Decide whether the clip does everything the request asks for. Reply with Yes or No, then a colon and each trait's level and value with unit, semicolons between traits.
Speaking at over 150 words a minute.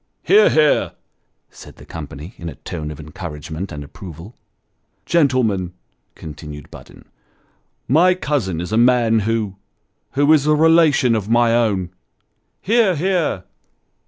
No: average, 145 wpm